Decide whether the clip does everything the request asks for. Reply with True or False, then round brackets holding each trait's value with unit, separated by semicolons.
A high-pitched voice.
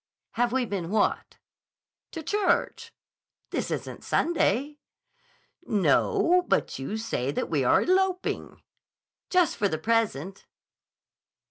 True (235 Hz)